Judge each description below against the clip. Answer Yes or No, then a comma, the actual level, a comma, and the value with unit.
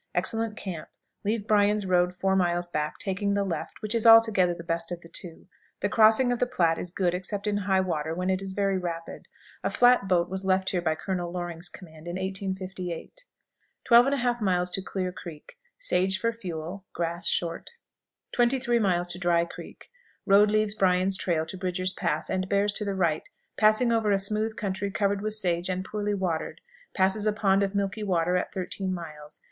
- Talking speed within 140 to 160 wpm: No, average, 185 wpm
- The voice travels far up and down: No, average, 2.9 semitones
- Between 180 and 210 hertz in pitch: Yes, high, 190 Hz